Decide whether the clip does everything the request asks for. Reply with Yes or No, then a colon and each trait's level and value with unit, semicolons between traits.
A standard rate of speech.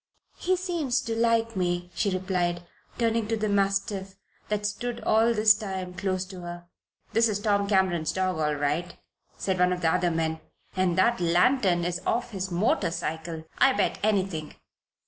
Yes: average, 170 wpm